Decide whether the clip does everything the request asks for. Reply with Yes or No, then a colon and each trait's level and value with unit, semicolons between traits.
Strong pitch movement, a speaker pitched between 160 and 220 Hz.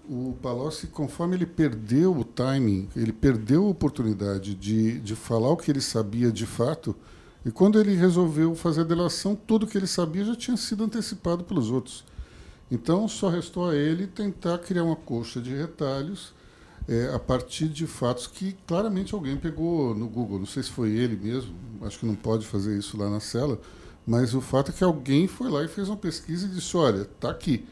No: wide, 7.0 semitones; medium, 140 Hz